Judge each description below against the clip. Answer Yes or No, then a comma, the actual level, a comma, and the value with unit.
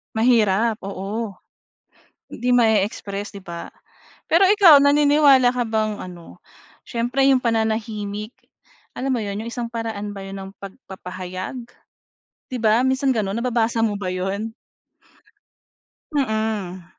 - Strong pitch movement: No, average, 3.7 semitones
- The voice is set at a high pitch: Yes, high, 220 Hz